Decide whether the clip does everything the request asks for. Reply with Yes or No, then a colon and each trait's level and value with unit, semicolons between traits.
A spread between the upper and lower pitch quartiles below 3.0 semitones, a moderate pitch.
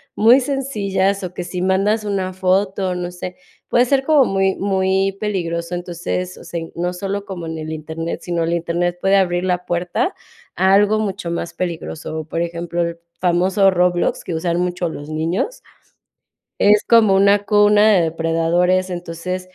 Yes: narrow, 2.6 semitones; medium, 180 Hz